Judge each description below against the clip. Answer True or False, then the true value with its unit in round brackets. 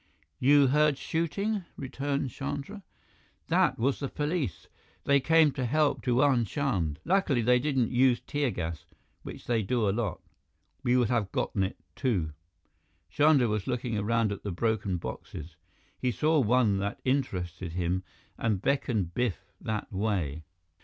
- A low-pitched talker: True (120 Hz)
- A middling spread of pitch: False (5.8 semitones)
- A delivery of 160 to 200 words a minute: False (145 wpm)